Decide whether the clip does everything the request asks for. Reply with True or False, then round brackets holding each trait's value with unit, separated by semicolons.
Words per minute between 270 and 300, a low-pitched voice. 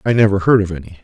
True (290 wpm; 100 Hz)